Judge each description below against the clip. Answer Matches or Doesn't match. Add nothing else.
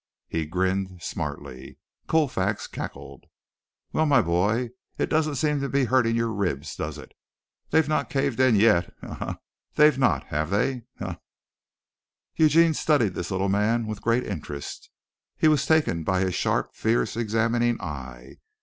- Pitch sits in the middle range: Doesn't match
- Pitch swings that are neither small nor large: Doesn't match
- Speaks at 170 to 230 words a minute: Doesn't match